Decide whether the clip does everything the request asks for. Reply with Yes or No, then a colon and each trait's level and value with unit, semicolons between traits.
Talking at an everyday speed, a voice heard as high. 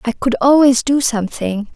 Yes: average, 170 wpm; high, 245 Hz